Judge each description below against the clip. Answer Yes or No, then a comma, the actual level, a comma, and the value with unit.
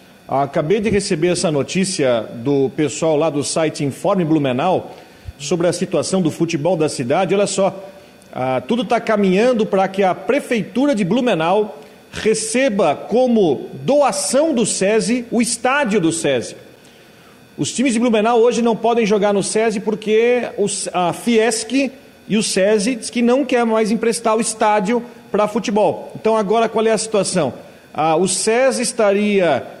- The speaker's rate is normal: Yes, average, 155 wpm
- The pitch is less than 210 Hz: No, high, 215 Hz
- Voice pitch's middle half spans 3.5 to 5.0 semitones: Yes, average, 4.3 semitones